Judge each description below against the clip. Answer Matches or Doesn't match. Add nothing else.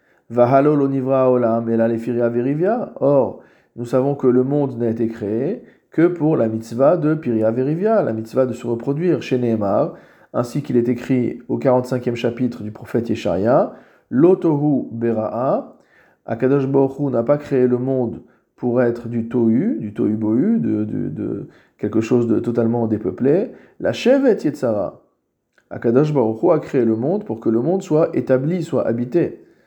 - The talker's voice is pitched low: Matches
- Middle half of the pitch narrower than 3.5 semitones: Matches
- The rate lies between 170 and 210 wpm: Doesn't match